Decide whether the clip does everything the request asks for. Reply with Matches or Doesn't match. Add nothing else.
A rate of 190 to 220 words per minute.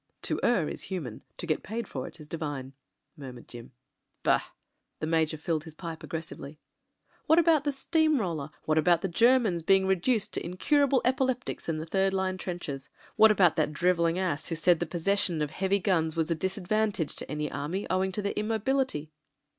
Matches